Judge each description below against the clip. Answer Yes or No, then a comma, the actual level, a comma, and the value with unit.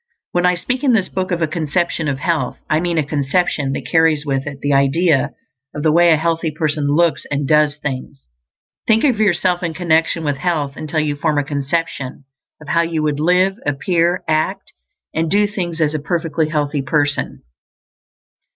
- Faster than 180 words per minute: Yes, average, 190 wpm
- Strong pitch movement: No, average, 3.0 semitones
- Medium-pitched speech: Yes, medium, 160 Hz